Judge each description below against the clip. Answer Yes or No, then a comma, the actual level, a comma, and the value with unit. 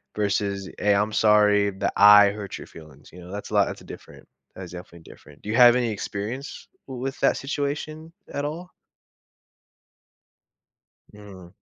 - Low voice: Yes, low, 105 Hz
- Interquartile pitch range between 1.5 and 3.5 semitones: No, average, 4.2 semitones